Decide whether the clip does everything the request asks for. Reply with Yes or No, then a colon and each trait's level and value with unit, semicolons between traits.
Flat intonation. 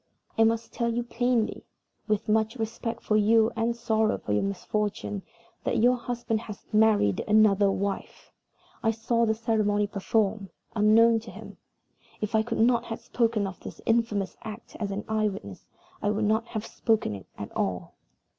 Yes: narrow, 1.8 semitones